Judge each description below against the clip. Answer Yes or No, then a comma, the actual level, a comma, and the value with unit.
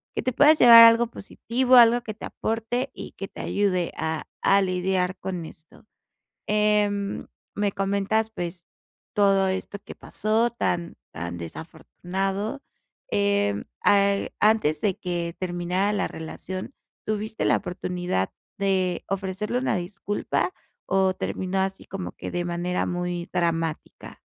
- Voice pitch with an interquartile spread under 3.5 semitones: Yes, average, 3.0 semitones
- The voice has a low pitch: No, high, 195 Hz